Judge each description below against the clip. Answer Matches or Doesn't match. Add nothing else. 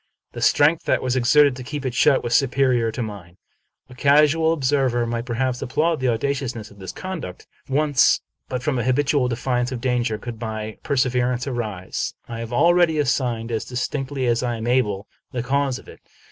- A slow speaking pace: Doesn't match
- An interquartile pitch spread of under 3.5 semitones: Matches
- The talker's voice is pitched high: Doesn't match